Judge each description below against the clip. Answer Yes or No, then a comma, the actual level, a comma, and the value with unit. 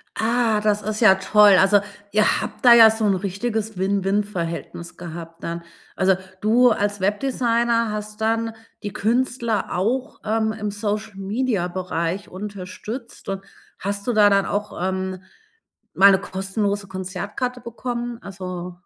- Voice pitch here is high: Yes, high, 205 Hz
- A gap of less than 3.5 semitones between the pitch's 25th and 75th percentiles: Yes, average, 2.8 semitones